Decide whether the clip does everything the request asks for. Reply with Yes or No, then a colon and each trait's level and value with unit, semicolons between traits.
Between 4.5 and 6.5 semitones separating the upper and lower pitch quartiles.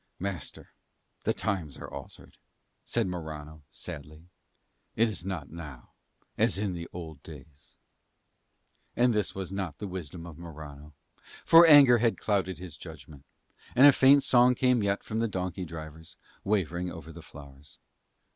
Yes: average, 5.1 semitones